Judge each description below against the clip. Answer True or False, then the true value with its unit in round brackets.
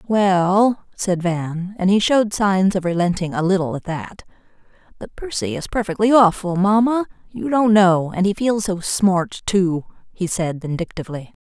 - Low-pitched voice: False (190 Hz)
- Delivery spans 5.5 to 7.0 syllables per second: False (4.6 syllables/s)